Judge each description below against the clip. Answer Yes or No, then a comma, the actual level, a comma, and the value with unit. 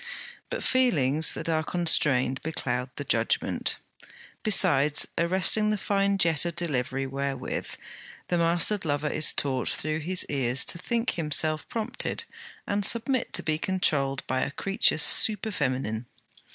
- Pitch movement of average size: No, wide, 5.7 semitones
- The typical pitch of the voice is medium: Yes, medium, 155 Hz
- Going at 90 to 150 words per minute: Yes, average, 140 wpm